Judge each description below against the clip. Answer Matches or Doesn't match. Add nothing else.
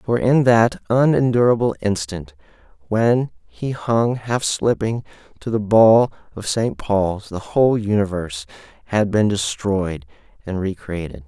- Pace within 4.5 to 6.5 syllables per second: Doesn't match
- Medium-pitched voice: Doesn't match